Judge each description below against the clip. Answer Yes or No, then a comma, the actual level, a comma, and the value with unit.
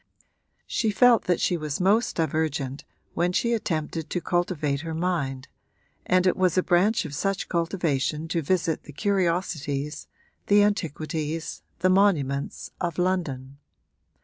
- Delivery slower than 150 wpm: Yes, slow, 135 wpm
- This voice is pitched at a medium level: Yes, medium, 170 Hz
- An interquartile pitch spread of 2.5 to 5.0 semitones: Yes, average, 3.8 semitones